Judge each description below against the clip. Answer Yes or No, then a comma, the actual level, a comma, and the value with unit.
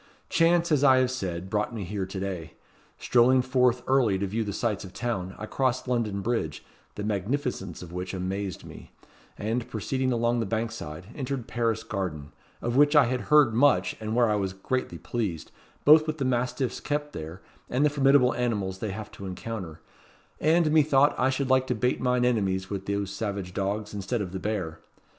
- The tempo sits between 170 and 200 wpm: Yes, average, 190 wpm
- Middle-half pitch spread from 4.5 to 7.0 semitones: Yes, average, 4.9 semitones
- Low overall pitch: Yes, low, 115 Hz